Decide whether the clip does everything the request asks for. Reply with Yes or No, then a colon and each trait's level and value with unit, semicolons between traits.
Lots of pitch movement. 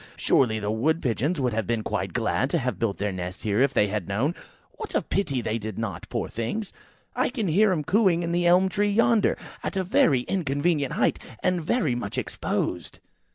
Yes: wide, 8.8 semitones